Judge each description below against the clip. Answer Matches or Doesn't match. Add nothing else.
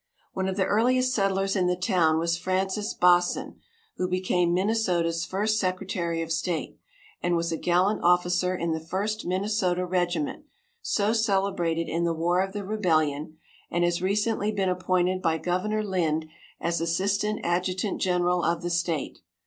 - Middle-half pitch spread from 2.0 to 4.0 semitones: Matches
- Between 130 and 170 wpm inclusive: Matches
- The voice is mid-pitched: Matches